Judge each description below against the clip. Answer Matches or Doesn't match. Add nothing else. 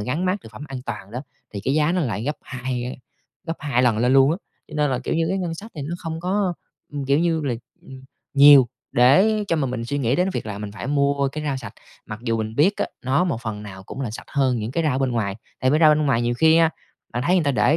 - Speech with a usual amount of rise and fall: Matches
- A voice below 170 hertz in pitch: Matches